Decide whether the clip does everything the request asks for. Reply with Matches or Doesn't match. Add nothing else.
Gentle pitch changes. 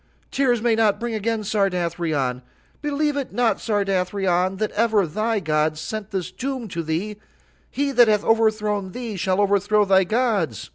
Doesn't match